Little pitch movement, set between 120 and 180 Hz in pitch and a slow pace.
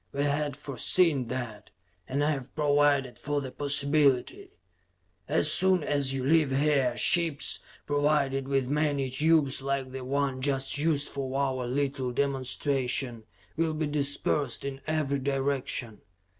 Yes: narrow, 1.8 semitones; medium, 140 Hz; slow, 130 wpm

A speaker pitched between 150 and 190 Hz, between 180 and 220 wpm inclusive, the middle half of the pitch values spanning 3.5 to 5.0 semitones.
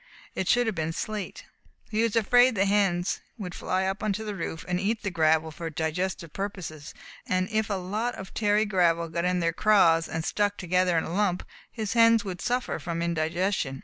Yes: medium, 185 Hz; average, 200 wpm; average, 3.9 semitones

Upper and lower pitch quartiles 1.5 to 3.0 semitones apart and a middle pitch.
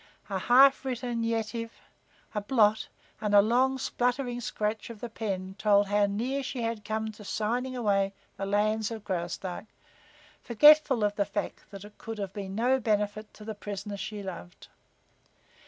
No: average, 2.7 semitones; high, 215 Hz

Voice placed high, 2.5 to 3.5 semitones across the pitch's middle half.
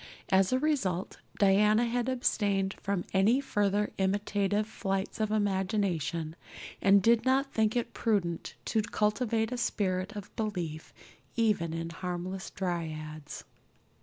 Yes: high, 200 Hz; average, 3.1 semitones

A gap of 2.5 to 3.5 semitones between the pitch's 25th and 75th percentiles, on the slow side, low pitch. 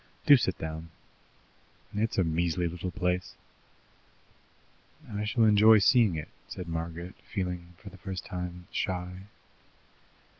Yes: average, 2.9 semitones; slow, 120 wpm; very low, 90 Hz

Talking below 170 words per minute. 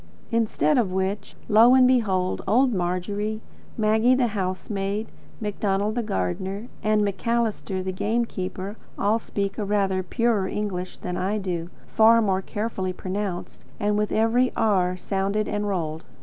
Yes: average, 145 wpm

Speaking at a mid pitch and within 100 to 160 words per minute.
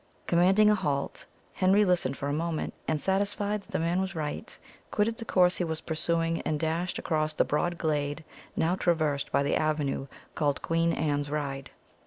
No: medium, 165 Hz; average, 180 wpm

